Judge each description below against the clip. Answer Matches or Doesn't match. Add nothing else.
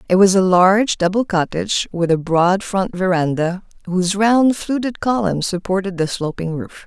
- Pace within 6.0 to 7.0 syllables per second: Doesn't match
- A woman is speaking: Matches